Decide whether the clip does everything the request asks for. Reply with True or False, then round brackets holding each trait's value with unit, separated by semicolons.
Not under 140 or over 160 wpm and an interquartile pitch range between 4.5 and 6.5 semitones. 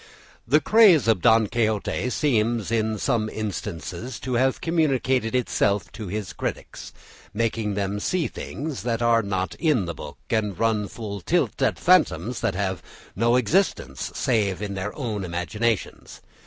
False (150 wpm; 3.7 semitones)